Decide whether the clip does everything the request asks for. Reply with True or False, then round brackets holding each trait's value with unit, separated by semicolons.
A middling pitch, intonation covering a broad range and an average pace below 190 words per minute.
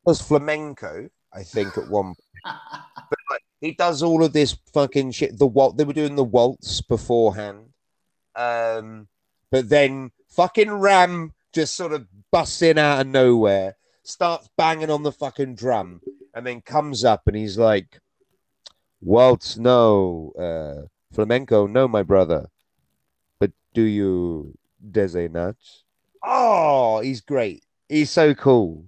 False (125 Hz; 6.5 semitones; 140 wpm)